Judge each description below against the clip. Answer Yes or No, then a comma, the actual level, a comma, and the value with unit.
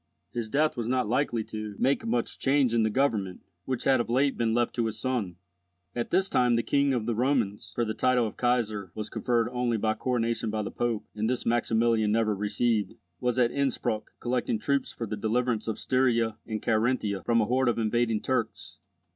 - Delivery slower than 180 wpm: No, fast, 205 wpm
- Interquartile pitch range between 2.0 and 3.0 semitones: Yes, narrow, 2.4 semitones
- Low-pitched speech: Yes, low, 115 Hz